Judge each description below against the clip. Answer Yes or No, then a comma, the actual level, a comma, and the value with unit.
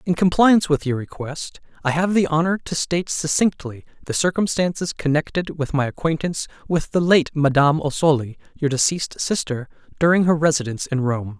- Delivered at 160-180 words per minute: Yes, average, 165 wpm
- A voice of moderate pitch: Yes, medium, 155 Hz